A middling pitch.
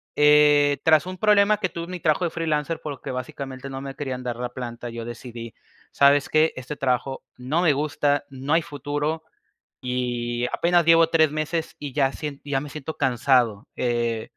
Yes: medium, 145 Hz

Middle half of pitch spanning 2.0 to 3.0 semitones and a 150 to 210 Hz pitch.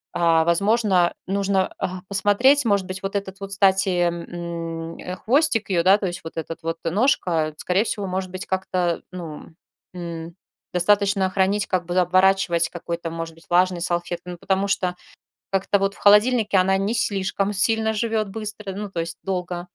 Yes: narrow, 2.6 semitones; high, 190 Hz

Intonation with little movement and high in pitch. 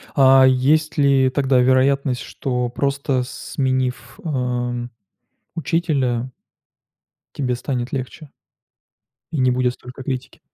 No: narrow, 1.8 semitones; low, 130 Hz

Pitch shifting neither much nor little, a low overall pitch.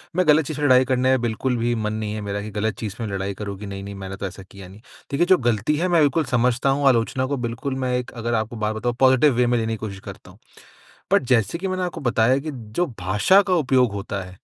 Yes: average, 4.4 semitones; low, 120 Hz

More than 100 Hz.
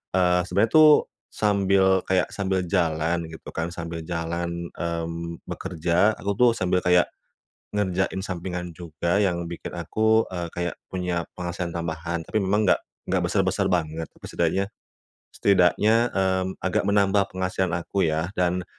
No: very low, 90 Hz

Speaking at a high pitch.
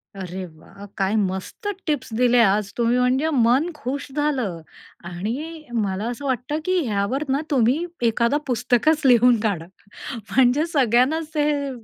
Yes: high, 245 Hz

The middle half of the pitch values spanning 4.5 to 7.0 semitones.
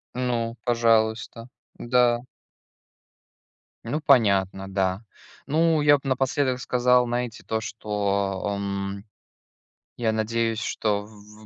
No: average, 3.4 semitones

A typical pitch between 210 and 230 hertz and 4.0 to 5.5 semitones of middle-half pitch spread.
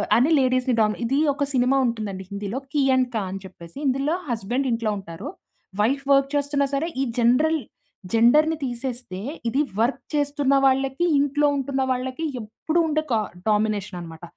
No: very high, 255 Hz; average, 4.3 semitones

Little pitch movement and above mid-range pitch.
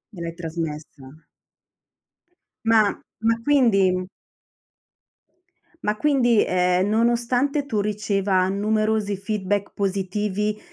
No: average, 3.2 semitones; high, 205 Hz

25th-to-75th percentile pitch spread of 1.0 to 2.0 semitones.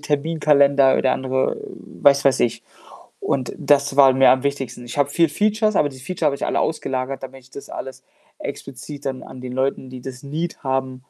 Yes: narrow, 1.7 semitones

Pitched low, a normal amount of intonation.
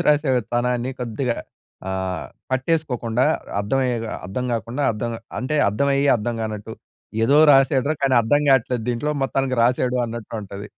Yes: low, 125 Hz; average, 3.2 semitones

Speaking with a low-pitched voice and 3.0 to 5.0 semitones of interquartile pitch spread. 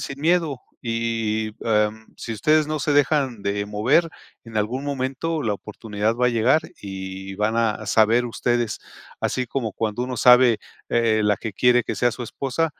Yes: low, 115 Hz; average, 3.5 semitones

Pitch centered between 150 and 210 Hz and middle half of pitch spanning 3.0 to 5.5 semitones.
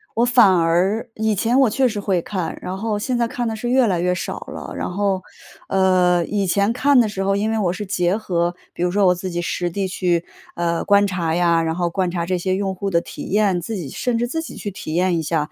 Yes: high, 190 Hz; average, 3.6 semitones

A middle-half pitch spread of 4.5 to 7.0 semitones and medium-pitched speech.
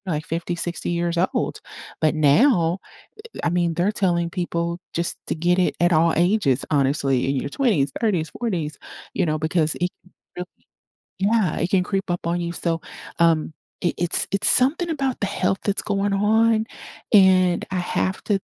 No: average, 3.1 semitones; medium, 175 Hz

